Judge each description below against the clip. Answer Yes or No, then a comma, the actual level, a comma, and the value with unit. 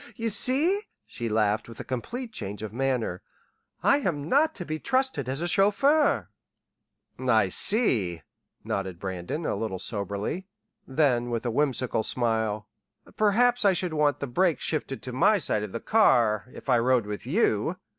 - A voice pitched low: Yes, low, 130 Hz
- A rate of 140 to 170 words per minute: Yes, average, 165 wpm